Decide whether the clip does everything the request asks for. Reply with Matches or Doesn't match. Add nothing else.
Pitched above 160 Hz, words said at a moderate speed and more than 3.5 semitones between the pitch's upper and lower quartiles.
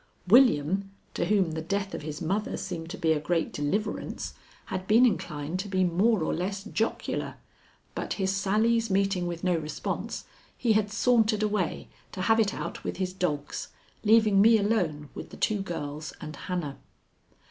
Matches